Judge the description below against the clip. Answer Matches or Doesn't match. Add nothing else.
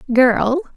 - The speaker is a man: Doesn't match